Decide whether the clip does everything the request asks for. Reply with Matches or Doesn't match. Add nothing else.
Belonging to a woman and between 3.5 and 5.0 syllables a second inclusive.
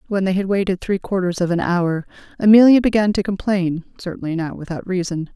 Doesn't match